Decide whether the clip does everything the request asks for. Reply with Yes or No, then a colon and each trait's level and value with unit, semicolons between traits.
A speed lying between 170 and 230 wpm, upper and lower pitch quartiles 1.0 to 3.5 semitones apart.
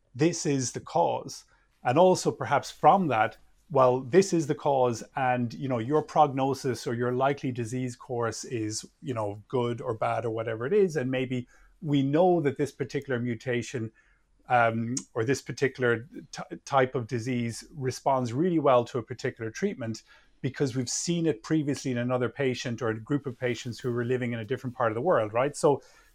Yes: average, 190 wpm; average, 3.0 semitones